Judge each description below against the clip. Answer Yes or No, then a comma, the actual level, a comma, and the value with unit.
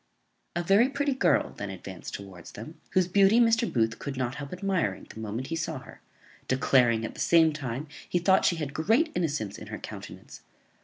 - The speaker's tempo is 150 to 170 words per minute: No, average, 195 wpm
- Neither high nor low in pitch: Yes, medium, 150 Hz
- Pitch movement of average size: No, wide, 8.5 semitones